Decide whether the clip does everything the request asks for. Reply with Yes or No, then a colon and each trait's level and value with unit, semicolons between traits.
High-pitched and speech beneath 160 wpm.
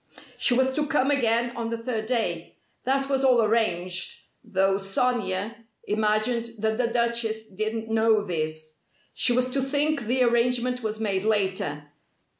Yes: high, 225 Hz; average, 150 wpm